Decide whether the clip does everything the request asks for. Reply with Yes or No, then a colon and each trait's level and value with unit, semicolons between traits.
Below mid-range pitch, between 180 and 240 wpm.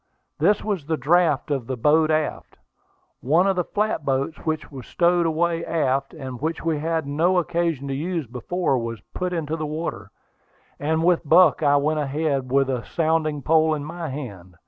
No: medium, 155 Hz; average, 190 wpm